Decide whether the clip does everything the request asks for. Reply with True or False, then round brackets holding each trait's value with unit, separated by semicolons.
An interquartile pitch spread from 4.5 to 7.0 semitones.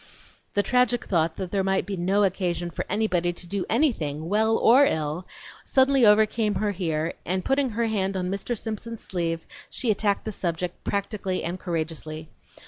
False (4.1 semitones)